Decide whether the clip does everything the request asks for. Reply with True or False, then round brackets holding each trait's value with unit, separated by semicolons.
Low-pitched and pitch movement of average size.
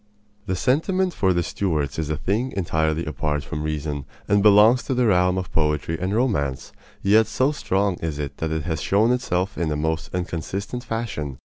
False (90 Hz; 5.7 semitones)